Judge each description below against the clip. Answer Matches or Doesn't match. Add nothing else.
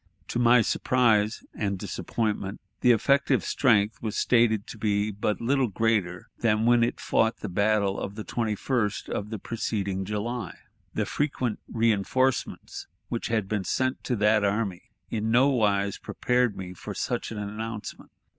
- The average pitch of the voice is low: Matches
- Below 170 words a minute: Matches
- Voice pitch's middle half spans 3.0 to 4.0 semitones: Doesn't match